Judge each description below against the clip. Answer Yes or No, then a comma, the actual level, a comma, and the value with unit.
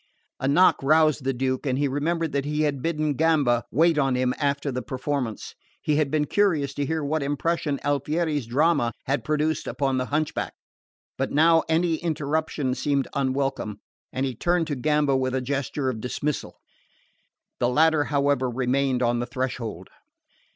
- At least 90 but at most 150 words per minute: No, average, 165 wpm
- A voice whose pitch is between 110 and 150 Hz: Yes, medium, 140 Hz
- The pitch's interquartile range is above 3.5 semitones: No, average, 2.9 semitones